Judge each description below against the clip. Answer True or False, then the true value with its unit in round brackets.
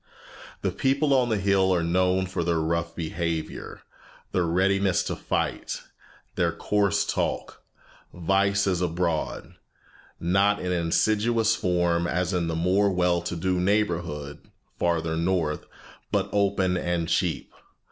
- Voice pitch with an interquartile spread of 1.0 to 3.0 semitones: True (2.6 semitones)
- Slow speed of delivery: True (130 wpm)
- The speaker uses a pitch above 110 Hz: False (90 Hz)